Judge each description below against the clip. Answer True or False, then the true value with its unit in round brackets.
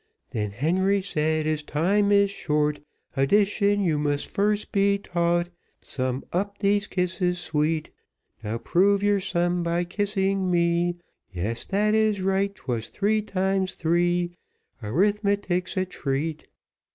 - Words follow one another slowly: True (125 wpm)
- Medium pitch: True (180 Hz)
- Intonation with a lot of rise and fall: False (4.2 semitones)